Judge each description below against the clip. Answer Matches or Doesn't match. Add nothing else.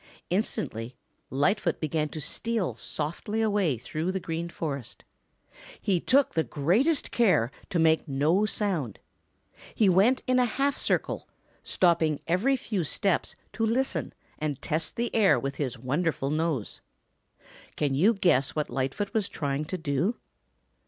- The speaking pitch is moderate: Matches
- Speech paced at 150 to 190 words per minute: Doesn't match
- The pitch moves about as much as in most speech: Doesn't match